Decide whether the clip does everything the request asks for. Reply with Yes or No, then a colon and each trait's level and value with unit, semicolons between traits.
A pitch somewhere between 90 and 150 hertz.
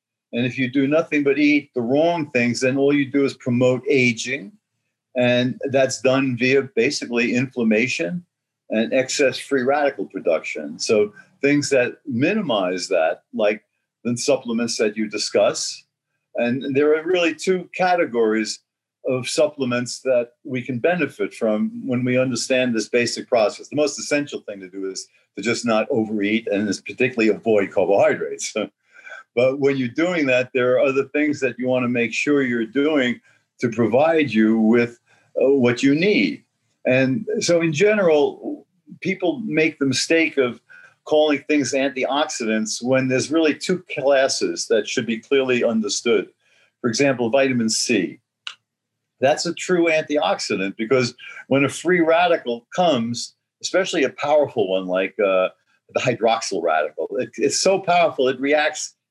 Yes: low, 135 Hz